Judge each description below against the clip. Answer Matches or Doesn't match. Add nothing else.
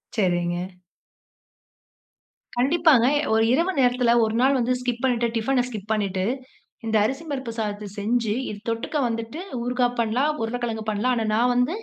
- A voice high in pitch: Matches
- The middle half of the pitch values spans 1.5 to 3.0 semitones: Matches